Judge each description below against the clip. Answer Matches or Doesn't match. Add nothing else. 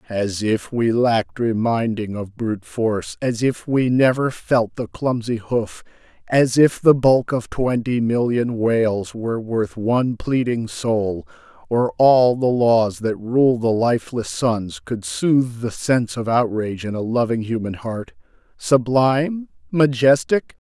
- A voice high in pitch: Doesn't match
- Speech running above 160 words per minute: Doesn't match